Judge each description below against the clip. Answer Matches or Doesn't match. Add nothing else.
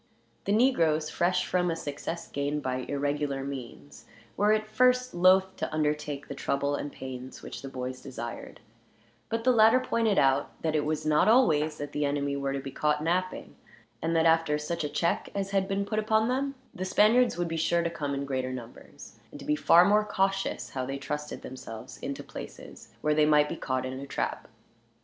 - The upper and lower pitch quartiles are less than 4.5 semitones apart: Doesn't match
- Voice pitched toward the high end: Doesn't match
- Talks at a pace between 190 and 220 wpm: Matches